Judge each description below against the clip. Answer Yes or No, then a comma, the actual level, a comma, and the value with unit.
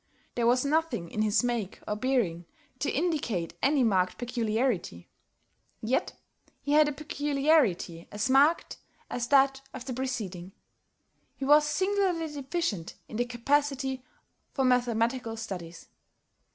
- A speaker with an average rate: No, slow, 125 wpm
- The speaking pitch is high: Yes, very high, 255 Hz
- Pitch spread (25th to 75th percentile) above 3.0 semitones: Yes, average, 5.0 semitones